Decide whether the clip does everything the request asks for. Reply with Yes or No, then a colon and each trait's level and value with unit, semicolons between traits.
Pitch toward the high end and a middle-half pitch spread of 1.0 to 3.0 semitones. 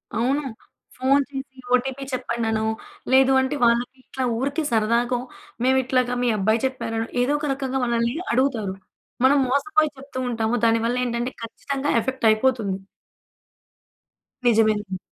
Yes: very high, 250 Hz; average, 2.7 semitones